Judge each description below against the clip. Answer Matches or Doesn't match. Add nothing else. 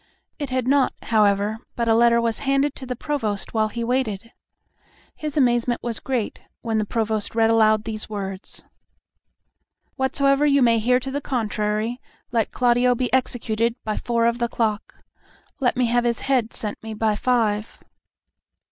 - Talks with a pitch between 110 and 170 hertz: Doesn't match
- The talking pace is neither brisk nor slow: Matches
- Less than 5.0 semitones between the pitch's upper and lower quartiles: Matches